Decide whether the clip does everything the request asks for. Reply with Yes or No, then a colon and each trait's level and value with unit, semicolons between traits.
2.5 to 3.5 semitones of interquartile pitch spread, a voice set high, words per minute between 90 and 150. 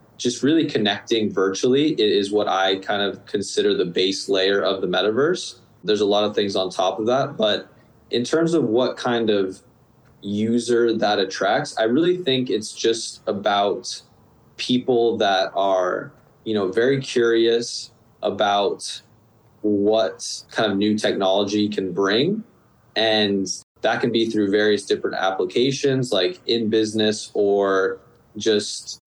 No: average, 3.0 semitones; low, 110 Hz; average, 140 wpm